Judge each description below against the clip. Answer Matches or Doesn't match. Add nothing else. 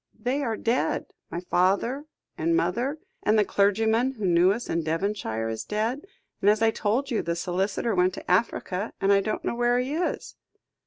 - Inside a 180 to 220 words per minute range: Matches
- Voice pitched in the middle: Doesn't match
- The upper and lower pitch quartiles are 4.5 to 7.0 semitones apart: Matches